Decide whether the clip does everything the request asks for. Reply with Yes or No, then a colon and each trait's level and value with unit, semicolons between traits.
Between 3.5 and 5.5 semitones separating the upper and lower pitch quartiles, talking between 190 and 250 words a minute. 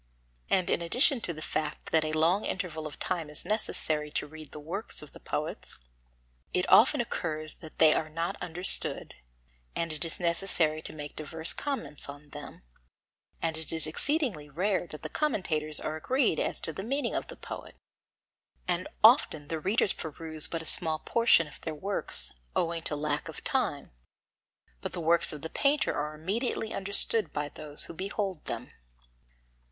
No: average, 4.0 semitones; average, 175 wpm